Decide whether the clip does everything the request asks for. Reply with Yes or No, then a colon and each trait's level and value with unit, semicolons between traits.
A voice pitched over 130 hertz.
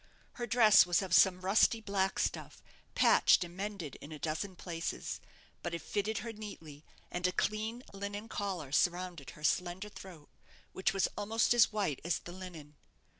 Yes: high, 190 Hz